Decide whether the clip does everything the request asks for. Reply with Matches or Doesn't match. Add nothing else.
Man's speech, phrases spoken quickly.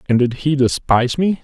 Matches